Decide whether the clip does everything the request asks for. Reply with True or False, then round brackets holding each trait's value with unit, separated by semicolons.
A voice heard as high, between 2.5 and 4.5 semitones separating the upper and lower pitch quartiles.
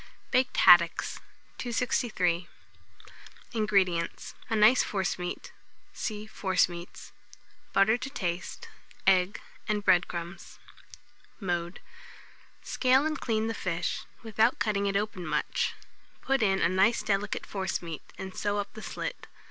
True (200 Hz; 3.6 semitones)